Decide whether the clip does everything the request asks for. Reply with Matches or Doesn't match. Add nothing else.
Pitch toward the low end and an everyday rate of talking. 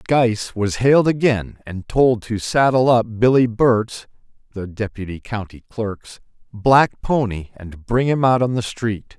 Matches